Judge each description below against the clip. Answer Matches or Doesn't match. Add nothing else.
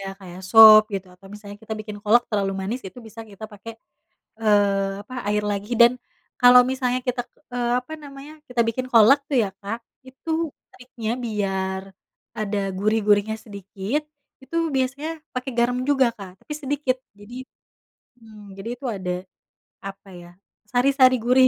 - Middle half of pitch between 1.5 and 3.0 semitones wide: Doesn't match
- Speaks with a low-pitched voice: Doesn't match